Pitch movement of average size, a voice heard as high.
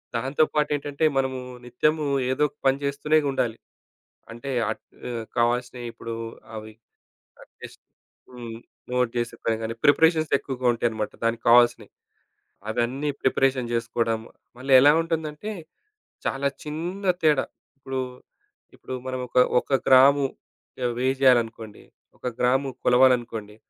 No: average, 3.2 semitones; low, 130 Hz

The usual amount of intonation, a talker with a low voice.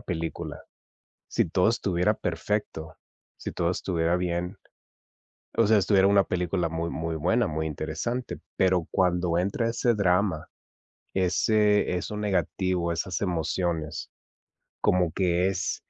Yes: average, 3.0 semitones; very low, 90 Hz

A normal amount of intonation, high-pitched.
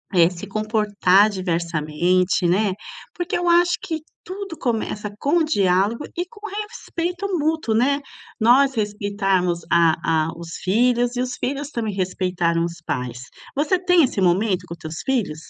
No: wide, 7.9 semitones; high, 210 Hz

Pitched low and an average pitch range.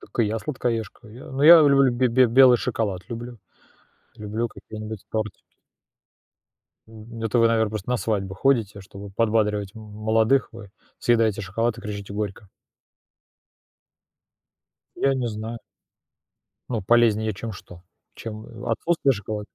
No: low, 110 Hz; narrow, 2.1 semitones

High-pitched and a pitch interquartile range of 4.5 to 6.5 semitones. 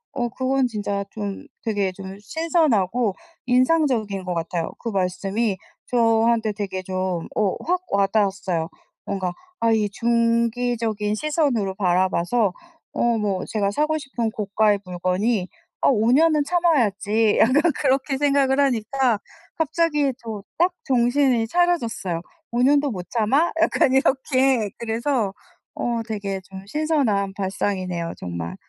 Yes: high, 225 Hz; average, 5.2 semitones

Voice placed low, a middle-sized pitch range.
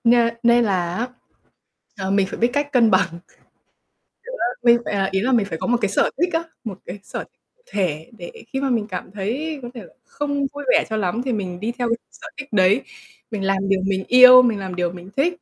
No: high, 215 Hz; average, 4.6 semitones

